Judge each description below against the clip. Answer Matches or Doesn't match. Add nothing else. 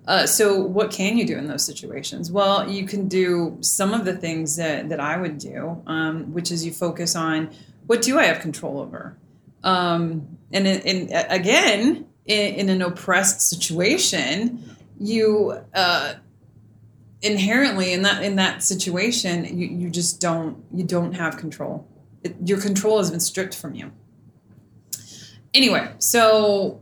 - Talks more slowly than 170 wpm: Matches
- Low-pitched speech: Doesn't match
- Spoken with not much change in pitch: Doesn't match